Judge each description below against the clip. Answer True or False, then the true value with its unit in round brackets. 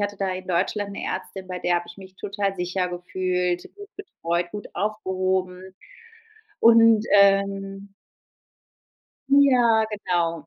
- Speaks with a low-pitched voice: False (190 Hz)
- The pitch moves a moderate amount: False (2.2 semitones)